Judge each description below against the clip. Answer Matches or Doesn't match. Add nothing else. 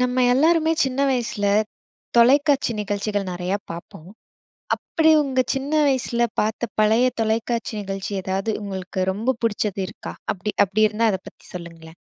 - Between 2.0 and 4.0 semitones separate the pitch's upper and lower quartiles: Doesn't match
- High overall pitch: Matches